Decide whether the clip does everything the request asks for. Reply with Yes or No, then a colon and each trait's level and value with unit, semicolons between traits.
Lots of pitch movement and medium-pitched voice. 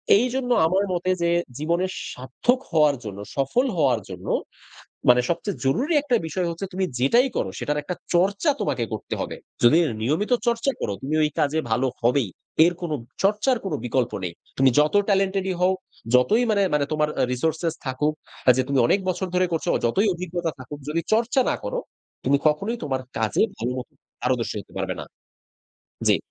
Yes: wide, 6.8 semitones; medium, 160 Hz